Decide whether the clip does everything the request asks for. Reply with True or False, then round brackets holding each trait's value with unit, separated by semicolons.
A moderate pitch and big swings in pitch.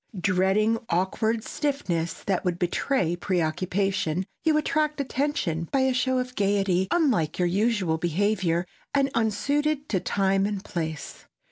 False (200 Hz; 6.5 semitones)